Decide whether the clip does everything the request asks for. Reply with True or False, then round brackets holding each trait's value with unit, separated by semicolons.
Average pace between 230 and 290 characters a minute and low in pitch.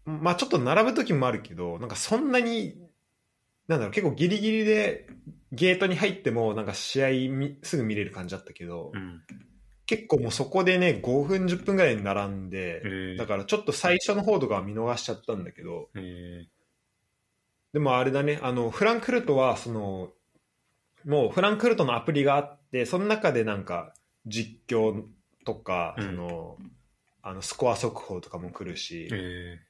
False (320 characters per minute; 125 Hz)